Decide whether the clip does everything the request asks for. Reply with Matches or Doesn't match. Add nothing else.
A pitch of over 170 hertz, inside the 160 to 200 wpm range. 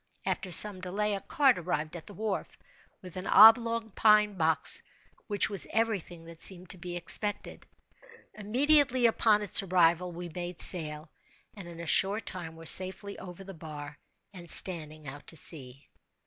Matches